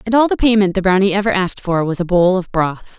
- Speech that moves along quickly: Yes, fast, 280 wpm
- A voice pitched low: No, high, 190 Hz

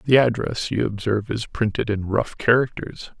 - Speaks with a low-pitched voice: Yes, low, 110 Hz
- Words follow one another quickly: No, average, 170 wpm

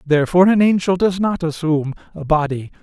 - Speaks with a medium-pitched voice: Yes, medium, 170 Hz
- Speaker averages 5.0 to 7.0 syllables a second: Yes, 6.2 syllables/s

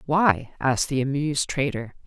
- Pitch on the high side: No, medium, 145 Hz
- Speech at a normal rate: Yes, average, 145 wpm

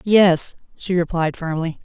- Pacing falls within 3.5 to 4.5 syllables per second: Yes, 4.0 syllables/s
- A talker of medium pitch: Yes, medium, 170 Hz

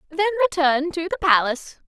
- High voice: Yes, very high, 325 Hz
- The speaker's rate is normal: Yes, average, 160 wpm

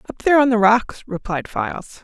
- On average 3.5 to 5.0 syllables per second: No, 5.6 syllables/s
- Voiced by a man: No, female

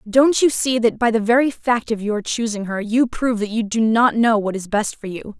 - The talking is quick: Yes, fast, 265 wpm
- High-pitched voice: Yes, high, 225 Hz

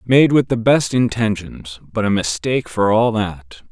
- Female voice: No, male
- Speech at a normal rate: Yes, average, 160 wpm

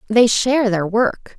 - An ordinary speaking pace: Yes, average, 175 wpm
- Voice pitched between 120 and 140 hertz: No, high, 225 Hz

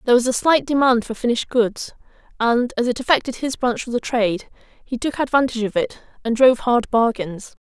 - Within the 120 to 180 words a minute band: No, fast, 205 wpm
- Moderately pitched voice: No, high, 245 Hz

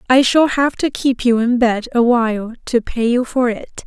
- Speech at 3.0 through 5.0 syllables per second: Yes, 4.8 syllables/s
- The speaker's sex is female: Yes, female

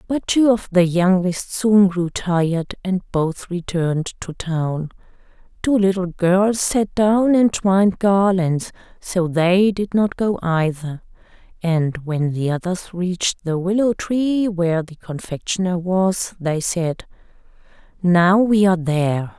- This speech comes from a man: No, female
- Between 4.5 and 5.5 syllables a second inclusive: No, 3.8 syllables/s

